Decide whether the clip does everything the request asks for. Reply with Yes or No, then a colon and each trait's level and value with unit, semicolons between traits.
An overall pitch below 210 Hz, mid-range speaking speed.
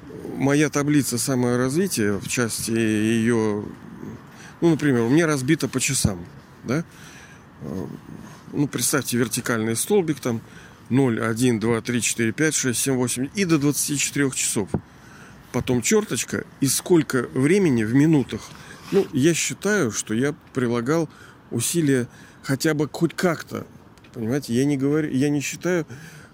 Yes: low, 135 Hz; average, 130 wpm